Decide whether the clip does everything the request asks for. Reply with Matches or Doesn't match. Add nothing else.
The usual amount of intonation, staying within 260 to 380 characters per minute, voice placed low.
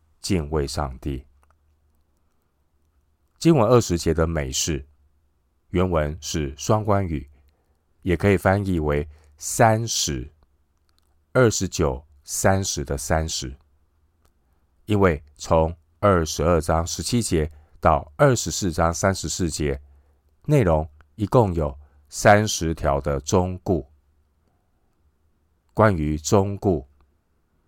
Doesn't match